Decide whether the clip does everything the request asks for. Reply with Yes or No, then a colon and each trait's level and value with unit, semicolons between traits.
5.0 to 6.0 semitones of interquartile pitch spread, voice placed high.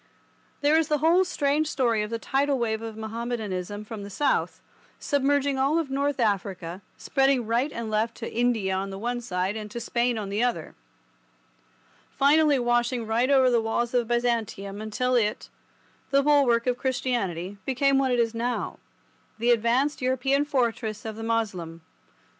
No: average, 3.8 semitones; high, 240 Hz